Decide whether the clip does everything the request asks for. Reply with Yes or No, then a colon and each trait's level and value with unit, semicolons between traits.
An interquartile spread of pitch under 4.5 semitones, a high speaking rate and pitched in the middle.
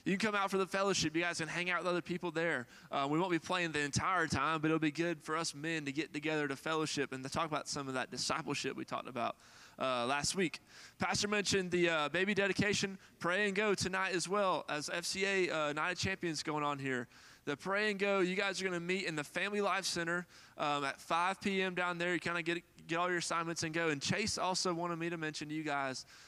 Yes: average, 3.7 semitones; fast, 255 wpm; medium, 170 Hz